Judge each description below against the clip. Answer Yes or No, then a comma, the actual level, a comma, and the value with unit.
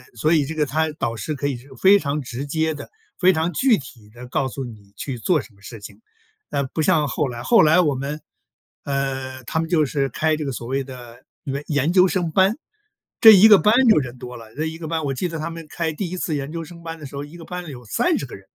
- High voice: No, medium, 150 Hz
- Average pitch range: Yes, average, 4.0 semitones